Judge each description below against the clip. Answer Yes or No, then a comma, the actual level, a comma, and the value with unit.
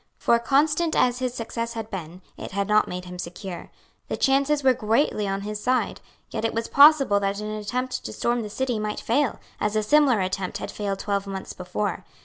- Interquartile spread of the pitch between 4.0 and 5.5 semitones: Yes, average, 4.3 semitones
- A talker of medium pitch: No, high, 215 Hz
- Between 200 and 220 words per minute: Yes, fast, 205 wpm